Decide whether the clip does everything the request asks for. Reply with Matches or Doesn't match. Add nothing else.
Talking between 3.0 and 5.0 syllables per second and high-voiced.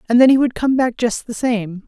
Doesn't match